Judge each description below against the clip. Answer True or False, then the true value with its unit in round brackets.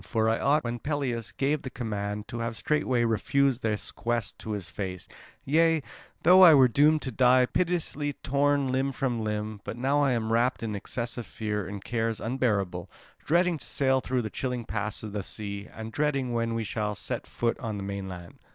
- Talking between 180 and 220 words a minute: True (195 wpm)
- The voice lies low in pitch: True (120 Hz)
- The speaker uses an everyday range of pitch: True (4.3 semitones)